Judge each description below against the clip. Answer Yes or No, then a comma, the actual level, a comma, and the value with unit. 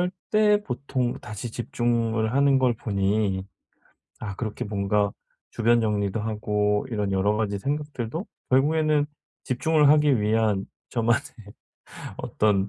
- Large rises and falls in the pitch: No, average, 4.6 semitones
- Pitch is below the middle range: Yes, low, 115 Hz